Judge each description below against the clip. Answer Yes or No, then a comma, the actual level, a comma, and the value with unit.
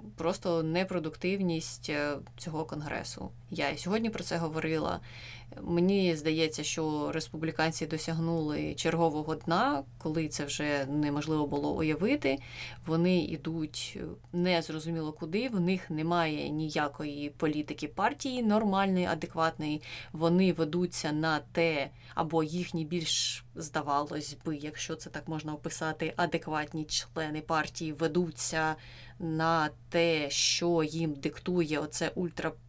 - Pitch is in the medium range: Yes, medium, 160 Hz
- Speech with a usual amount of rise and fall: No, narrow, 2.0 semitones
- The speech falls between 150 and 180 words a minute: No, average, 110 wpm